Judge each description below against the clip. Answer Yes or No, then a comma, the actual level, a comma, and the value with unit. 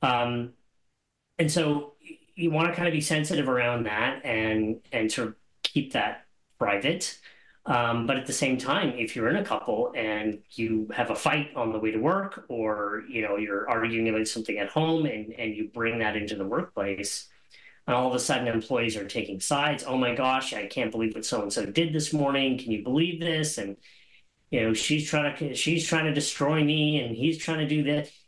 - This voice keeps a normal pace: No, fast, 210 wpm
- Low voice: Yes, low, 130 Hz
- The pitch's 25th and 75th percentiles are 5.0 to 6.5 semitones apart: Yes, wide, 5.5 semitones